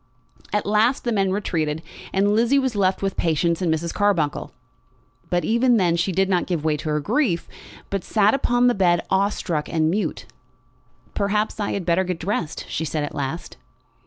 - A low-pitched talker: No, high, 190 Hz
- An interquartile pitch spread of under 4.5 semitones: Yes, average, 3.9 semitones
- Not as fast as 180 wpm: No, average, 190 wpm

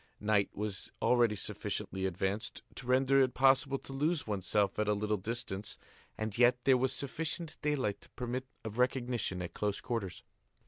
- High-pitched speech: No, low, 120 Hz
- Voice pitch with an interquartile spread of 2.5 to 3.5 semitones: No, average, 4.3 semitones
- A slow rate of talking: No, average, 165 wpm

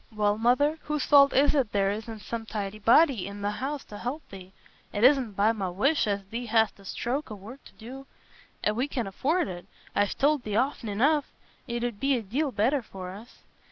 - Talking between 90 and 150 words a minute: No, fast, 205 wpm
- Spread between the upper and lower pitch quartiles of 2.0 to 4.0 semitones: No, average, 5.0 semitones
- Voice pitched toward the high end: Yes, high, 230 Hz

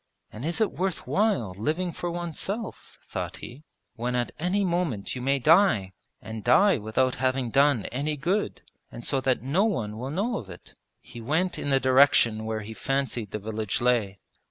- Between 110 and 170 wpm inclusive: No, average, 180 wpm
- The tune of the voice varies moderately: No, wide, 7.3 semitones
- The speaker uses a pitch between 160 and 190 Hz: No, low, 130 Hz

